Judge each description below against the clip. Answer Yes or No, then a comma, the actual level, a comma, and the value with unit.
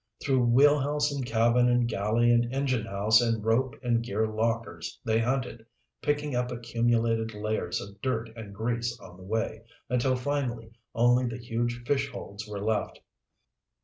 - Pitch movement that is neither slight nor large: No, narrow, 2.0 semitones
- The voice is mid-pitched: No, low, 115 Hz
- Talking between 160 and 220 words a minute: No, average, 150 wpm